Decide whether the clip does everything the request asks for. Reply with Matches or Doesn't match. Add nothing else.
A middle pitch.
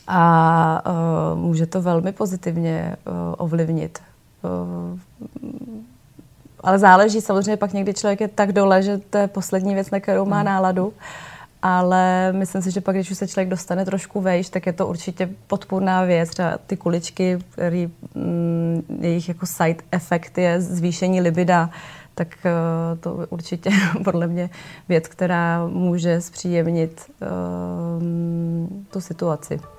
Matches